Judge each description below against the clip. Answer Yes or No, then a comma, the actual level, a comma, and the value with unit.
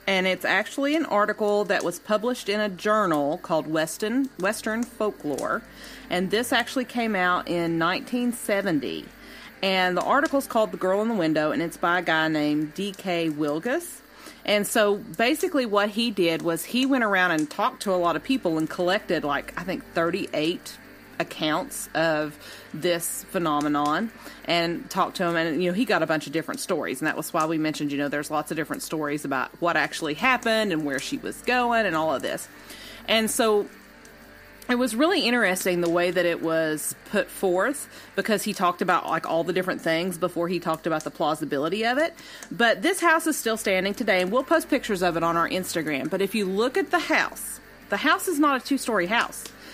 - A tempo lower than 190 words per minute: No, average, 200 wpm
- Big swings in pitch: Yes, wide, 5.9 semitones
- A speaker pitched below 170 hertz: No, high, 190 Hz